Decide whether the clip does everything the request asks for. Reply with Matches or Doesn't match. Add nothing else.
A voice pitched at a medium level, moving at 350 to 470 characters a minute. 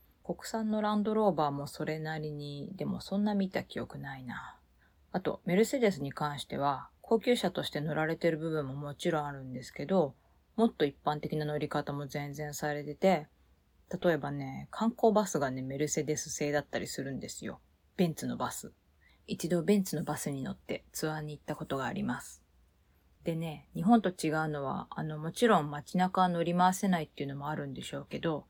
Matches